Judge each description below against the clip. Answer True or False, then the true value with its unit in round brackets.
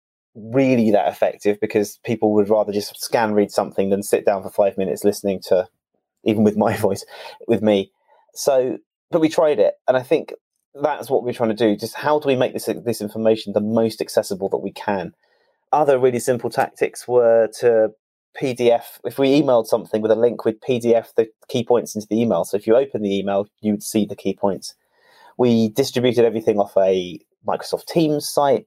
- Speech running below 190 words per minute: False (195 wpm)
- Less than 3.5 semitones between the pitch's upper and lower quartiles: True (3.0 semitones)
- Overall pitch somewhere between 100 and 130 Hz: True (110 Hz)